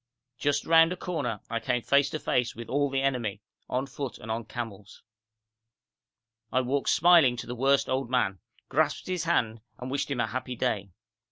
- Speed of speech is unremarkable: Yes, average, 185 wpm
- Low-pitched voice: Yes, low, 130 Hz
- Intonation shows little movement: No, average, 3.4 semitones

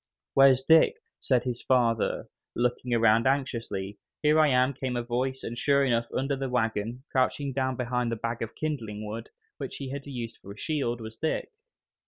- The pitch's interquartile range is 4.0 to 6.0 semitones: No, average, 2.7 semitones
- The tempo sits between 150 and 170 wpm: No, average, 185 wpm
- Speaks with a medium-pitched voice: No, low, 125 Hz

